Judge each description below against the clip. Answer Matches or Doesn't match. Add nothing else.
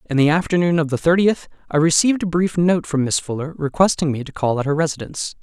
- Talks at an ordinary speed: Doesn't match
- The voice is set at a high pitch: Doesn't match